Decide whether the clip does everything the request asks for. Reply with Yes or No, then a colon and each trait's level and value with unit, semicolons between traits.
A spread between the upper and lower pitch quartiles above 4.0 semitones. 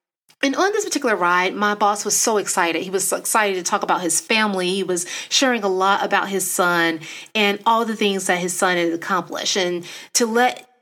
No: average, 3.7 semitones